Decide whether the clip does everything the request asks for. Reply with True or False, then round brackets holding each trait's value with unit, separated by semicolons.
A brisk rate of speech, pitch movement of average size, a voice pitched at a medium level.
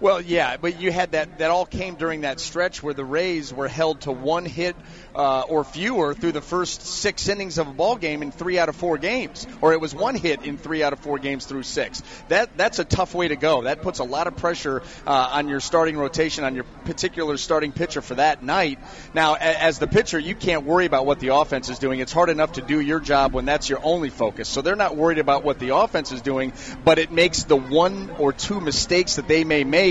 True (245 wpm; 3.4 semitones; 155 Hz)